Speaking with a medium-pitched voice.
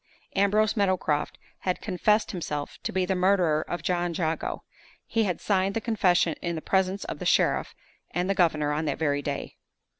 Yes: medium, 180 Hz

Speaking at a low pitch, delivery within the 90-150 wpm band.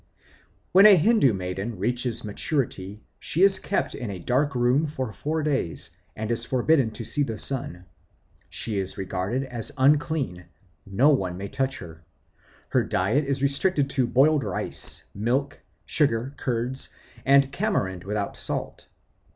Yes: low, 125 Hz; average, 145 wpm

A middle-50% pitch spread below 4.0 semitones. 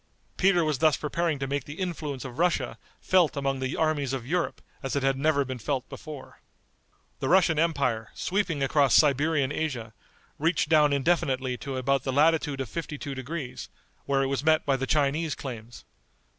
Yes: average, 2.9 semitones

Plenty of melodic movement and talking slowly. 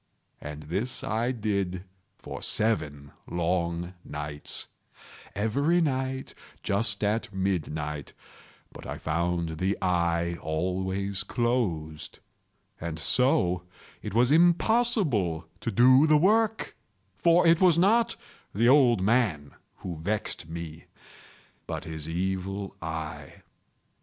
Yes: wide, 7.1 semitones; slow, 100 wpm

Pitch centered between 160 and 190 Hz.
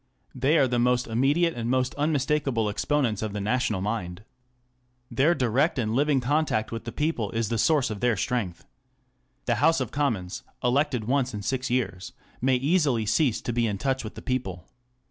No: low, 125 Hz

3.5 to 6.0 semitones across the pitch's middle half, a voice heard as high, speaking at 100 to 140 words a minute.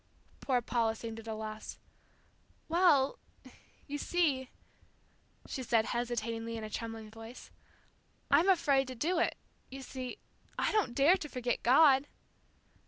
Yes: average, 4.0 semitones; very high, 255 Hz; slow, 135 wpm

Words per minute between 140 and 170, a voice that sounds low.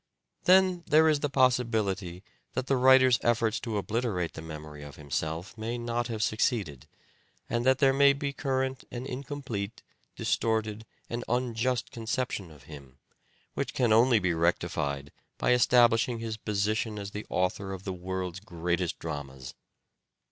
Yes: average, 150 wpm; low, 110 Hz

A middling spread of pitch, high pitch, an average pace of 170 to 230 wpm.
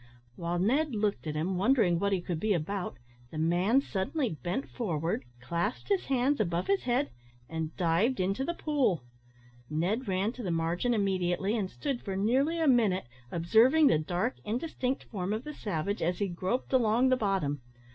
No: wide, 6.4 semitones; high, 200 Hz; average, 175 wpm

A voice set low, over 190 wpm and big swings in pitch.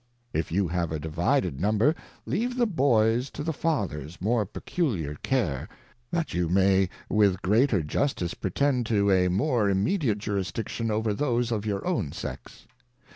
No: low, 105 Hz; average, 155 wpm; wide, 6.2 semitones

